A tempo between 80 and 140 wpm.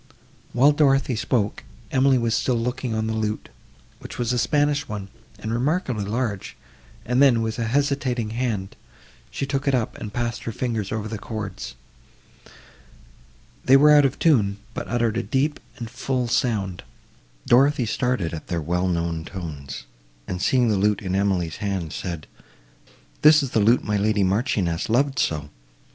No: average, 165 wpm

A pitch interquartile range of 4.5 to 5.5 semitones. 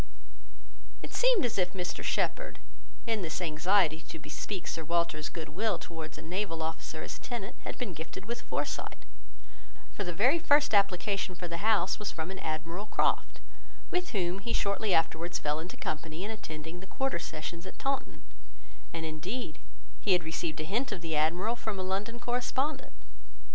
Yes: average, 5.1 semitones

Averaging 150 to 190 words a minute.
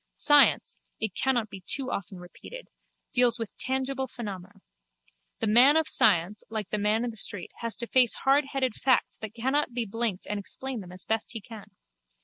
Yes: average, 180 wpm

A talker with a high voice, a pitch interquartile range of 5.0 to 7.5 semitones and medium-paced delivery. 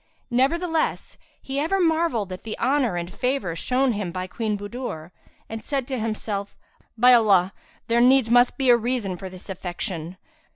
Yes: high, 230 Hz; wide, 5.5 semitones; average, 165 wpm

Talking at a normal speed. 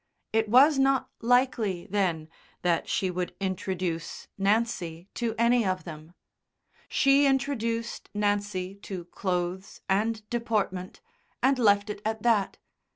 No: slow, 120 wpm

